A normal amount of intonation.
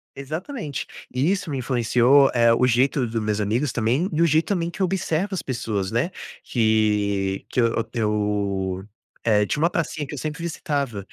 No: wide, 6.2 semitones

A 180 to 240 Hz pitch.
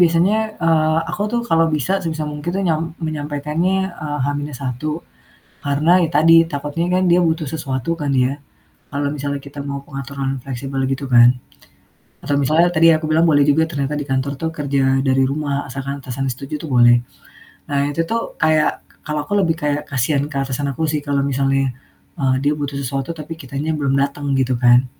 No: medium, 145 Hz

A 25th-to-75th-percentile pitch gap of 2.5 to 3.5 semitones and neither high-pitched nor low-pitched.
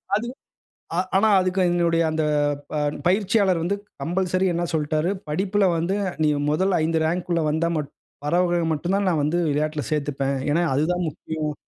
Yes: average, 3.2 semitones; medium, 170 Hz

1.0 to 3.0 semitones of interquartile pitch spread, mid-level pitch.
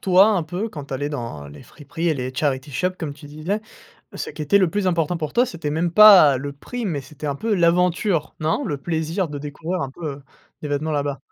No: average, 3.9 semitones; medium, 155 Hz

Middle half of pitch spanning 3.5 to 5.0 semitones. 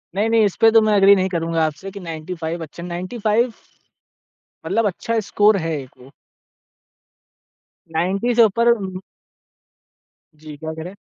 Yes: average, 4.7 semitones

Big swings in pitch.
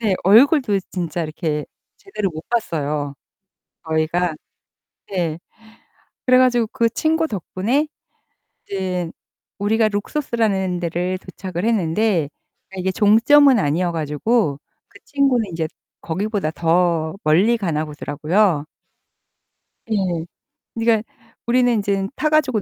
Yes: wide, 5.8 semitones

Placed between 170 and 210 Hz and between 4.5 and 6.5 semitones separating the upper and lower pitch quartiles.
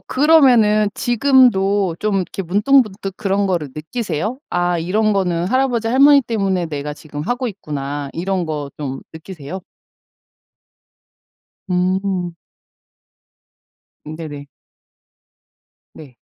Yes: high, 190 Hz; wide, 5.5 semitones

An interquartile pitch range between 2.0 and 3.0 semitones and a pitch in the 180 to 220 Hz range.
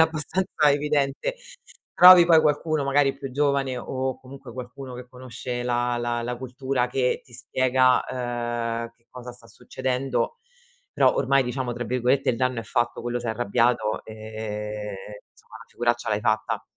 No: narrow, 2.4 semitones; low, 125 Hz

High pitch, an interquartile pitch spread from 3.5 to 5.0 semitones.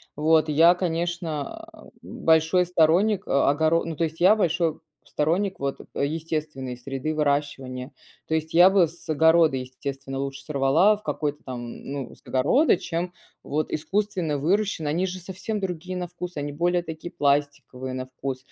No: medium, 160 Hz; average, 3.8 semitones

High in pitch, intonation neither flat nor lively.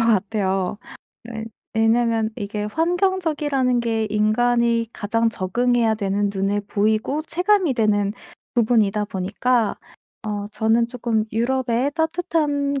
Yes: high, 230 Hz; average, 3.3 semitones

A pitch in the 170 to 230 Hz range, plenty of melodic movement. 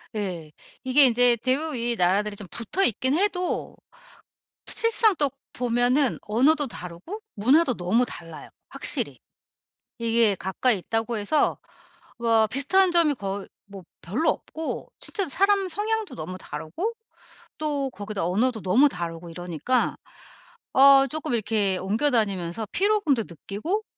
No: high, 240 Hz; wide, 7.1 semitones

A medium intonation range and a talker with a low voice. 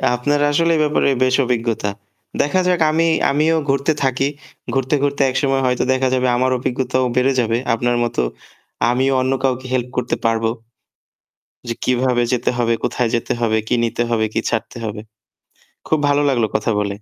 No: narrow, 2.3 semitones; low, 130 Hz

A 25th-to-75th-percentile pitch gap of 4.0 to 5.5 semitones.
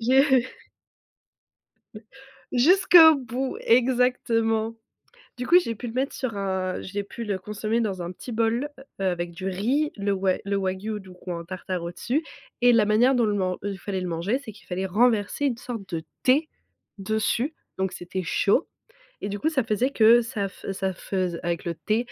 Yes: average, 4.6 semitones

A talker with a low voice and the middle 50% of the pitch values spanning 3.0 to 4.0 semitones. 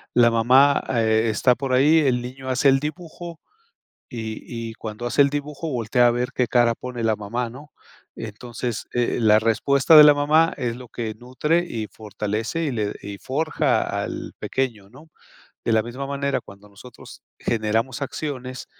Yes: low, 125 Hz; average, 3.7 semitones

